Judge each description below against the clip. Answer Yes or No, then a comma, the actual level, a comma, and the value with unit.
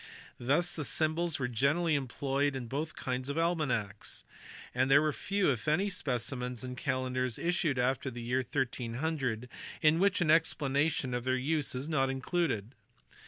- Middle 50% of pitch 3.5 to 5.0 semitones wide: Yes, average, 3.9 semitones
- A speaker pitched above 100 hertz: Yes, low, 135 Hz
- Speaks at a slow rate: No, average, 160 wpm